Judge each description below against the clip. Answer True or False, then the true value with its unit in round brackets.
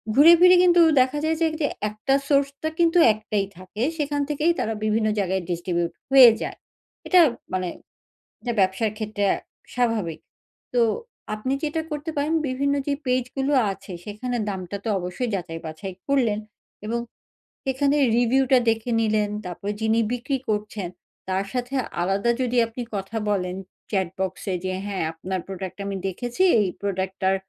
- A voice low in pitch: False (220 Hz)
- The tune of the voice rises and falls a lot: True (5.9 semitones)